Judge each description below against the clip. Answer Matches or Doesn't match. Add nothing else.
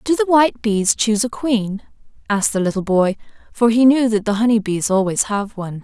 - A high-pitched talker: Matches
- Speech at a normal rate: Doesn't match